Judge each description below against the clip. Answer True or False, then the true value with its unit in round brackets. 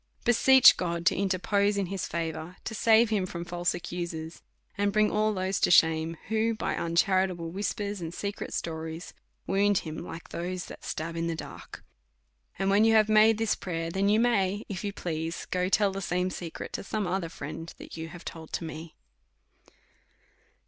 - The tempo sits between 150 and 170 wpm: False (185 wpm)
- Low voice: False (185 Hz)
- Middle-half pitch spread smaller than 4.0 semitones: True (3.5 semitones)